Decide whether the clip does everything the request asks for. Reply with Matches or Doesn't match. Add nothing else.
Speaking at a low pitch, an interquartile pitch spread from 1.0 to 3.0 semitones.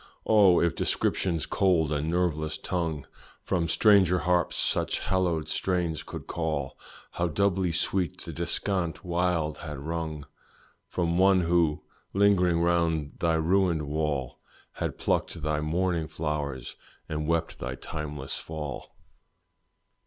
Matches